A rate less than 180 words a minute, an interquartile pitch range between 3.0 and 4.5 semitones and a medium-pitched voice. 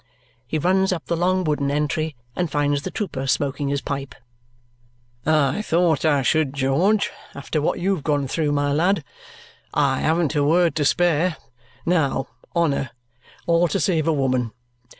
Yes: average, 160 wpm; average, 3.5 semitones; medium, 155 Hz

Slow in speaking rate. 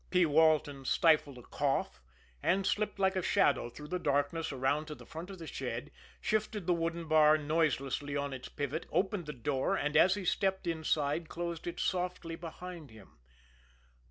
No: average, 175 wpm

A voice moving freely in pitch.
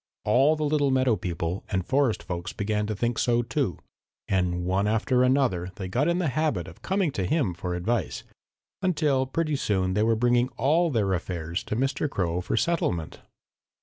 Yes: wide, 7.0 semitones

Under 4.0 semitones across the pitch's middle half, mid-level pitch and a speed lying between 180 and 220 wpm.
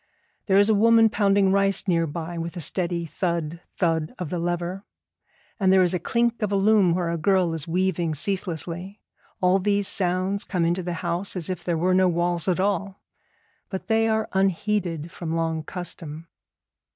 Yes: average, 2.7 semitones; medium, 180 Hz; average, 185 wpm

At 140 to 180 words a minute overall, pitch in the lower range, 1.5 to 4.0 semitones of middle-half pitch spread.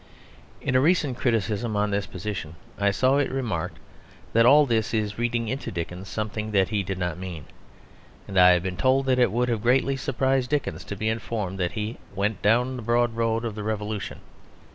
No: average, 200 wpm; low, 110 Hz; average, 3.6 semitones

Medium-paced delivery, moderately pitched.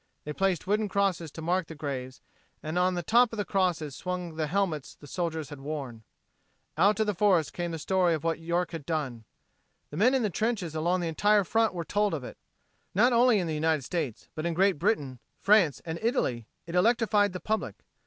No: fast, 215 wpm; medium, 175 Hz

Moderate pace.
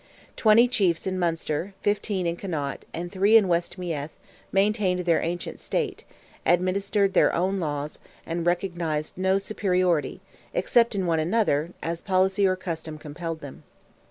Yes: average, 145 wpm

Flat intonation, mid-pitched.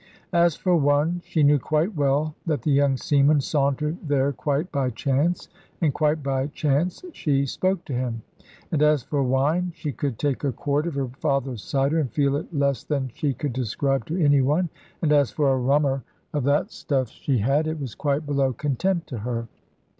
Yes: narrow, 2.3 semitones; medium, 145 Hz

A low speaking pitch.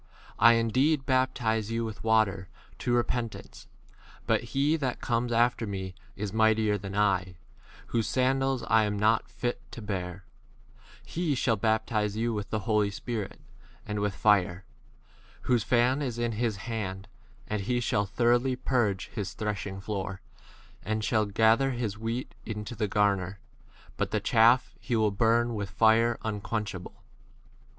Yes: low, 110 Hz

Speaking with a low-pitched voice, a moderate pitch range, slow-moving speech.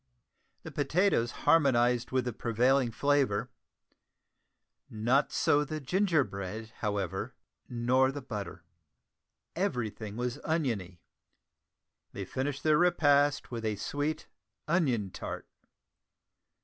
Yes: low, 125 Hz; average, 4.7 semitones; slow, 100 wpm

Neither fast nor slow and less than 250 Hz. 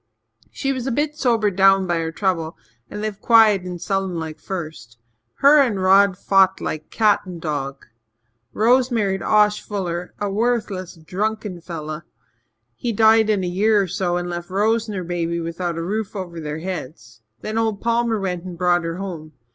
Yes: average, 185 wpm; high, 190 Hz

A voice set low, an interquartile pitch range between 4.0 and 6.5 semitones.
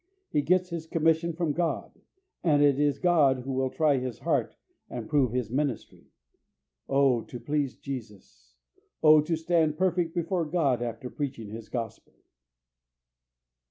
No: medium, 145 Hz; average, 4.5 semitones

